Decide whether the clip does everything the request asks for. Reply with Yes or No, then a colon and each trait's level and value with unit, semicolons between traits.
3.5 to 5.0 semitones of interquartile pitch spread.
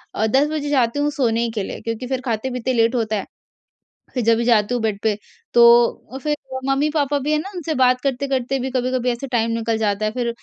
No: average, 2.9 semitones